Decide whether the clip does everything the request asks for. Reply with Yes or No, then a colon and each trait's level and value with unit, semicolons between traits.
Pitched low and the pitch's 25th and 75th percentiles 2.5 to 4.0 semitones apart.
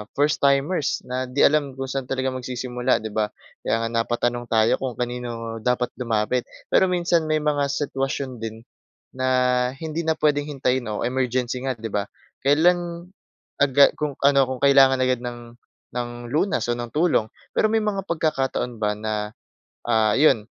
Yes: low, 130 Hz; average, 3.3 semitones